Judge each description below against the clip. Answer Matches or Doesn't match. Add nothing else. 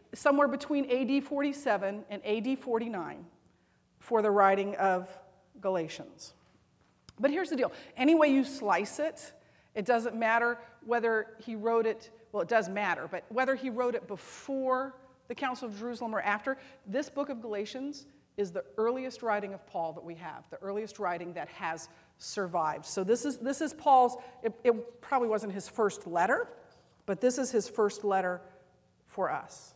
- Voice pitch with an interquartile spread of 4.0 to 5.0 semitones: Matches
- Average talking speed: Matches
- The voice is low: Doesn't match